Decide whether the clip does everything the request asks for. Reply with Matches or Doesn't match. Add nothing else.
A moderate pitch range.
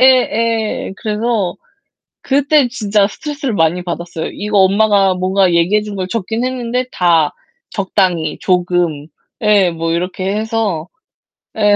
Matches